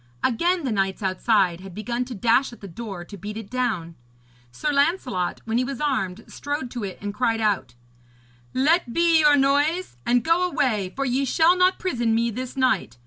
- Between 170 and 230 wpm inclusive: Yes, average, 195 wpm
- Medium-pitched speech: No, high, 240 Hz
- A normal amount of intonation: No, wide, 5.8 semitones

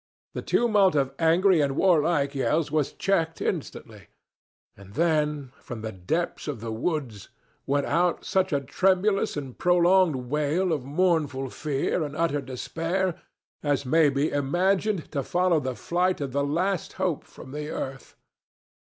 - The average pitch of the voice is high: No, medium, 150 Hz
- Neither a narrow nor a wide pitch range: Yes, average, 4.4 semitones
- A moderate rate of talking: Yes, average, 150 wpm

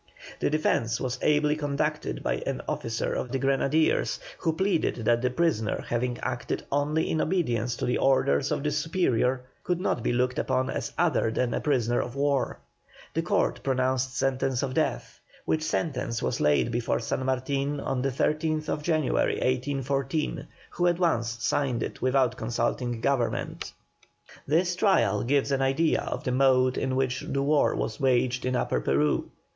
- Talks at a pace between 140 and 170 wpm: Yes, average, 165 wpm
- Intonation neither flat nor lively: Yes, average, 3.4 semitones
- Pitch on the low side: Yes, low, 130 Hz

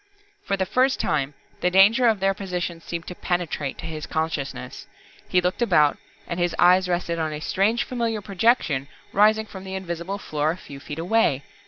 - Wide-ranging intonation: No, average, 3.8 semitones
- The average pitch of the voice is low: No, medium, 180 Hz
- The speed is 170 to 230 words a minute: Yes, average, 185 wpm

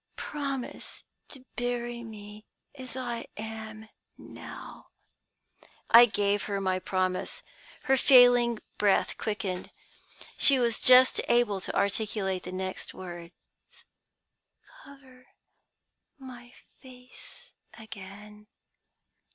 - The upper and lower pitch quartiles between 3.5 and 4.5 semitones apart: Yes, average, 3.8 semitones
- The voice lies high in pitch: Yes, high, 225 Hz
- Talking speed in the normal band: No, slow, 95 wpm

